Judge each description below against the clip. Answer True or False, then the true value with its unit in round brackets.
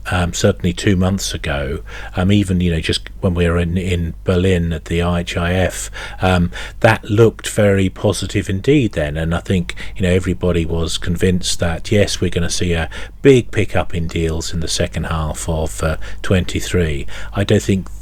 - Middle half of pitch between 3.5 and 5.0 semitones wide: False (2.7 semitones)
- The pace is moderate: True (185 wpm)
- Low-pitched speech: True (90 Hz)